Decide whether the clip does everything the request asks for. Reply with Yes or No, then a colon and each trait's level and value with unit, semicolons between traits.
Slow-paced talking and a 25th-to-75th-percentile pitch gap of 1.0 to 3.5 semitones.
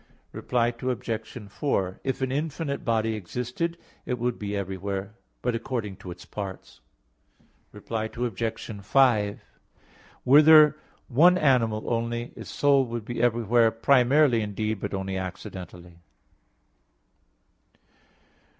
No: slow, 115 wpm; average, 4.0 semitones